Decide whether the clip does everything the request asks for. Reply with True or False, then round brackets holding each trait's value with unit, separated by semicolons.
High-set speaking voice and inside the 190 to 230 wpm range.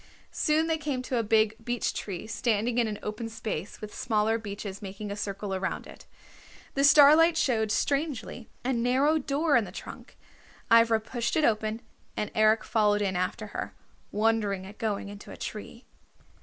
False (225 Hz; 170 wpm)